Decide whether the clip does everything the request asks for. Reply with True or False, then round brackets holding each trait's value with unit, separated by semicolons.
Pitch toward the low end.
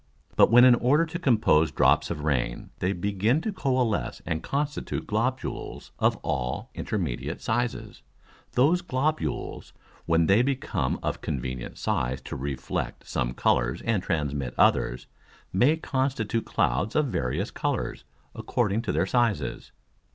True (105 Hz)